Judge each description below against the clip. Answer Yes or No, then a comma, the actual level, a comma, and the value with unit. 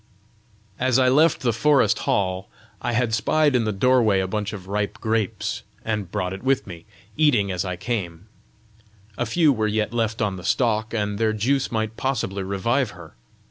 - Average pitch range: Yes, average, 4.0 semitones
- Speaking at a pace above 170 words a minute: Yes, average, 180 wpm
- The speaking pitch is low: Yes, low, 110 Hz